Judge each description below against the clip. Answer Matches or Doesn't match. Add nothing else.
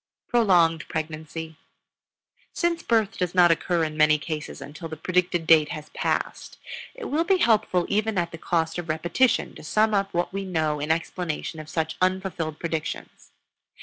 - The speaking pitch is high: Doesn't match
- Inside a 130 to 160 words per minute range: Doesn't match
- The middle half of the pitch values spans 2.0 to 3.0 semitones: Doesn't match